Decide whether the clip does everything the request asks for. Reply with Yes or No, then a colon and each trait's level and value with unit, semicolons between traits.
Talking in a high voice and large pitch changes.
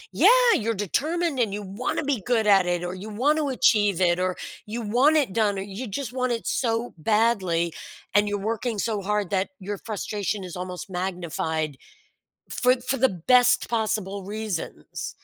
No: high, 210 Hz; average, 4.2 semitones